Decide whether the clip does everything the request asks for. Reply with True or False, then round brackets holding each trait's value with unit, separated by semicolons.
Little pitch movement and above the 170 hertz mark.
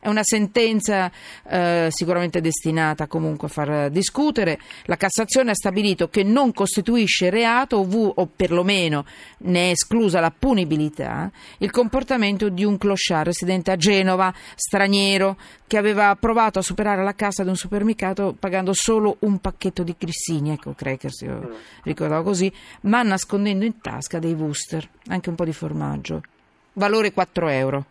False (3.7 semitones; 190 Hz)